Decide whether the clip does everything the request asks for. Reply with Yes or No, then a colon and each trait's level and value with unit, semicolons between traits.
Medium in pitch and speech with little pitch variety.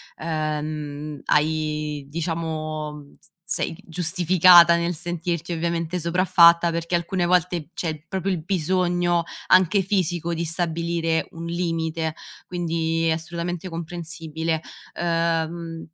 Yes: medium, 170 Hz; narrow, 1.5 semitones